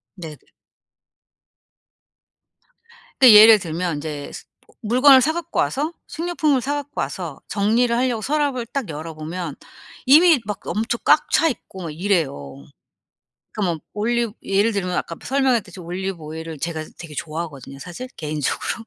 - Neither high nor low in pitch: No, high, 205 Hz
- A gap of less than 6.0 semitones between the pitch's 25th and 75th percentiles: No, wide, 7.9 semitones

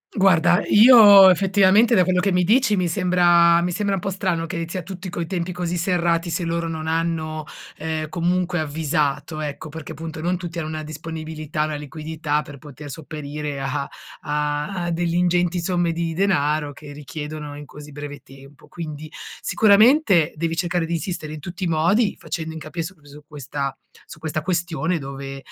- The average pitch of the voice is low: No, medium, 165 Hz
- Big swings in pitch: No, average, 2.9 semitones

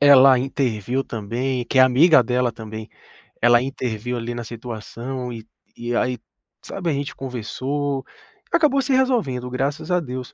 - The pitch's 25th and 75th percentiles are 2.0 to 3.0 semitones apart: Yes, average, 2.7 semitones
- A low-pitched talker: Yes, low, 125 Hz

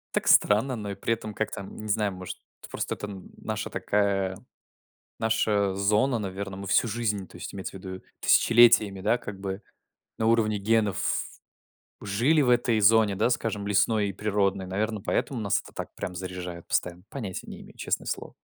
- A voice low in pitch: Yes, low, 105 Hz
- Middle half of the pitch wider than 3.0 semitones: No, narrow, 2.4 semitones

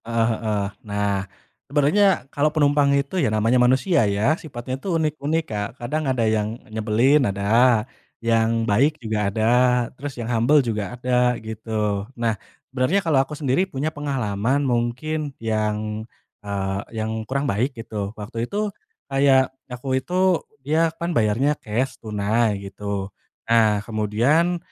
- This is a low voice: Yes, low, 120 Hz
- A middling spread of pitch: Yes, average, 4.8 semitones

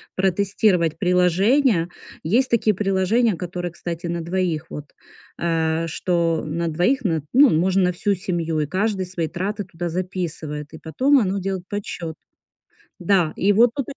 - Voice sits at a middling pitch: Yes, medium, 180 Hz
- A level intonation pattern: No, average, 3.2 semitones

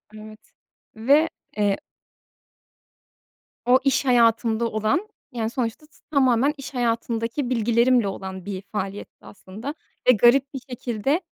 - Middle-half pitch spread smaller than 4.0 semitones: Yes, average, 3.3 semitones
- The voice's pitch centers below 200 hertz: No, high, 235 Hz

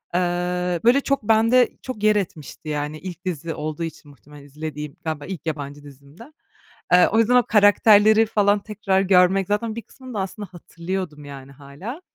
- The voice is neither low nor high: Yes, medium, 180 Hz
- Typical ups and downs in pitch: No, wide, 5.8 semitones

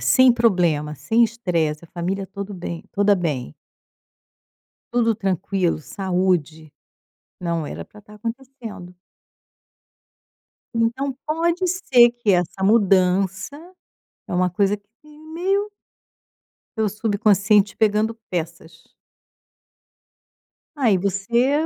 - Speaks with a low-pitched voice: No, high, 200 Hz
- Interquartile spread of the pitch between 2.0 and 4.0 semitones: No, average, 4.6 semitones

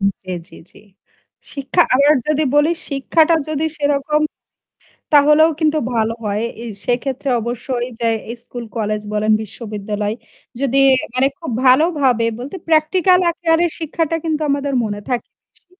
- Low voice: No, very high, 275 Hz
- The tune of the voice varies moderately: Yes, average, 5.0 semitones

